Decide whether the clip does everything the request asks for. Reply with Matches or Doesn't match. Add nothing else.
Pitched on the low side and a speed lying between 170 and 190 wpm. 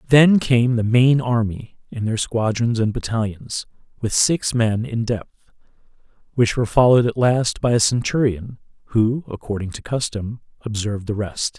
Doesn't match